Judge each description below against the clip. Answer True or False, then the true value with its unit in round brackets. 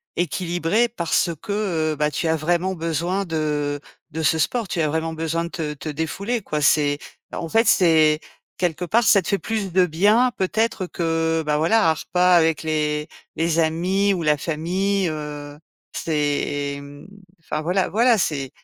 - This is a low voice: False (165 Hz)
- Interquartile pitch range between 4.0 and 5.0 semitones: False (3.6 semitones)